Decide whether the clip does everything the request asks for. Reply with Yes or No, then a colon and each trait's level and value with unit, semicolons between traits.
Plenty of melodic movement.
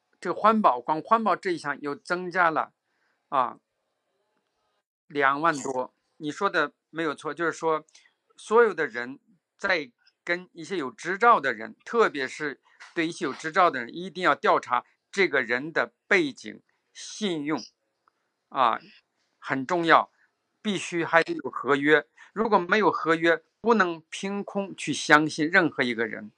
No: average, 4.8 semitones